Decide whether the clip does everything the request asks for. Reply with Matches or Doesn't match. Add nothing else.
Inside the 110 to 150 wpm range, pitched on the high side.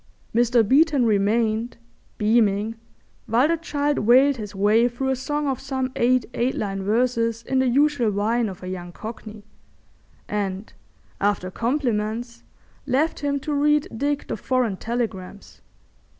Matches